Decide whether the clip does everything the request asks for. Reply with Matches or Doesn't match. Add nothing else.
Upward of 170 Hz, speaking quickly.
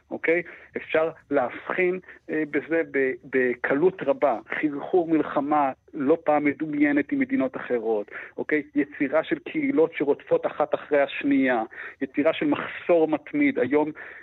Doesn't match